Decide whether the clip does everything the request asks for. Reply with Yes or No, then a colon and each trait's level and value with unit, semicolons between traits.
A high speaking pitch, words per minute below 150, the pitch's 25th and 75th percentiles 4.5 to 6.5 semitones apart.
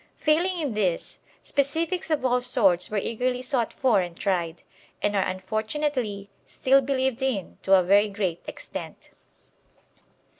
Yes: high, 230 Hz; average, 140 wpm; wide, 5.5 semitones